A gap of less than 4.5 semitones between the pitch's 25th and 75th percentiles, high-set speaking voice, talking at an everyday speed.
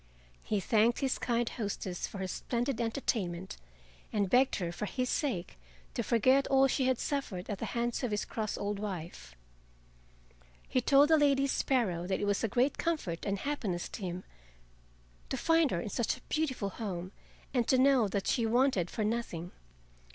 No: wide, 5.4 semitones; high, 225 Hz; average, 180 wpm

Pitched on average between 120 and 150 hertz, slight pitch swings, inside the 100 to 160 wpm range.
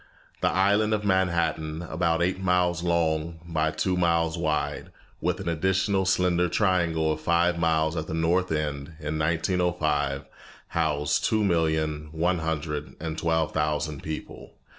No: very low, 80 Hz; narrow, 2.2 semitones; average, 140 wpm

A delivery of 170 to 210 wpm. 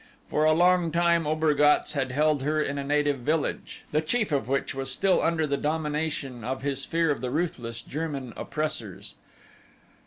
Yes: average, 175 wpm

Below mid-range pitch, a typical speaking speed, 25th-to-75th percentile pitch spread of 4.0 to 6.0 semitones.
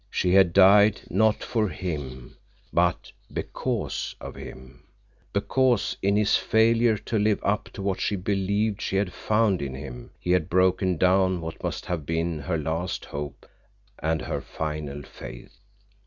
Yes: very low, 95 Hz; average, 150 wpm; average, 4.5 semitones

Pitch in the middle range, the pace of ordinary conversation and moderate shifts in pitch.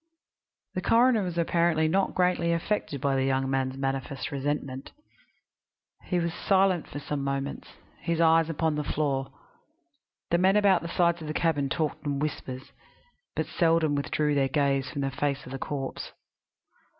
Yes: medium, 150 Hz; average, 160 wpm; average, 3.7 semitones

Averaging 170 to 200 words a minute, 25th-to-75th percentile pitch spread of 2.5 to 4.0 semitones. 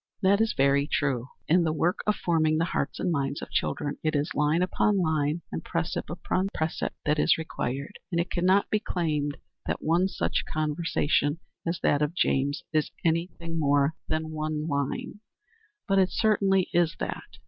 Yes: average, 180 wpm; average, 3.1 semitones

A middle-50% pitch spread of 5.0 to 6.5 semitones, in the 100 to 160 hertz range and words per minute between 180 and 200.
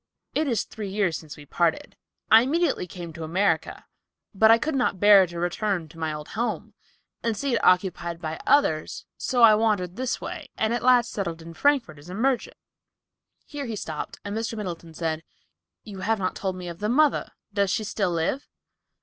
No: average, 5.3 semitones; high, 200 Hz; average, 195 wpm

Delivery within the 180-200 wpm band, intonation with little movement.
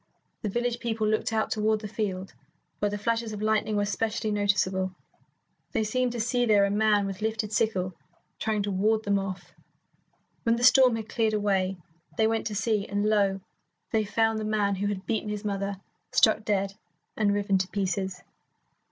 Yes: average, 185 wpm; narrow, 1.8 semitones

